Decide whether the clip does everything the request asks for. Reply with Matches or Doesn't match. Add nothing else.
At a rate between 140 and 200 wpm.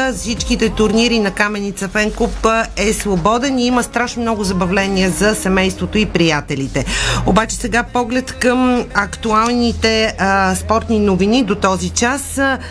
Doesn't match